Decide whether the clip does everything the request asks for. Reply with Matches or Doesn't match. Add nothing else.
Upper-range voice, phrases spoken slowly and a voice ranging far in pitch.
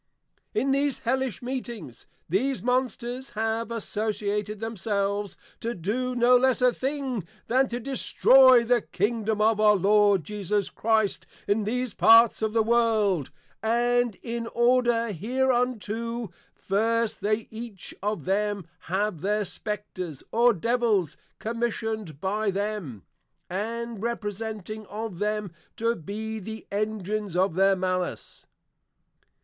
Doesn't match